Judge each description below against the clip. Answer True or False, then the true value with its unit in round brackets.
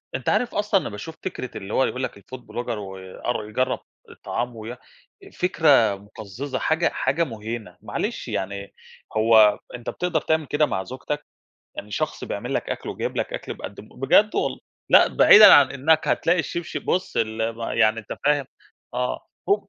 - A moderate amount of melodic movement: False (6.6 semitones)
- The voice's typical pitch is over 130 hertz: False (125 Hz)